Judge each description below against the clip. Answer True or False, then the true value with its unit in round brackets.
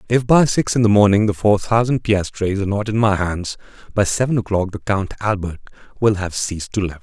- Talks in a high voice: False (105 Hz)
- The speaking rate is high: True (220 wpm)